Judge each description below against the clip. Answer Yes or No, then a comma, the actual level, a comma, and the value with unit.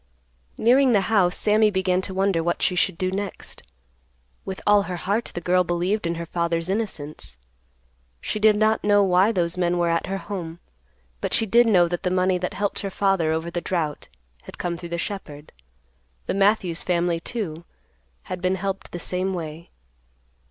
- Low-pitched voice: No, medium, 185 Hz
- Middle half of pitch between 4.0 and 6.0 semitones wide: No, average, 2.8 semitones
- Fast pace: No, average, 185 wpm